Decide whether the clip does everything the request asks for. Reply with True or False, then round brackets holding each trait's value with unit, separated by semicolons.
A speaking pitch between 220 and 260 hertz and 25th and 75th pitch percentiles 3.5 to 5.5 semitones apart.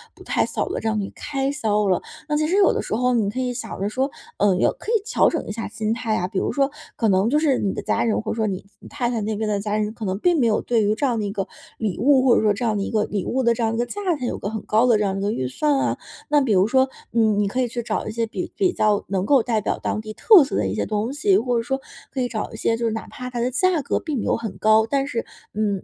True (225 Hz; 3.9 semitones)